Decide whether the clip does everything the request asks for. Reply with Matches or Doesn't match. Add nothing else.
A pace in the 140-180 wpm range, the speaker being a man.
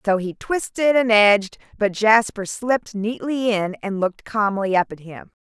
Doesn't match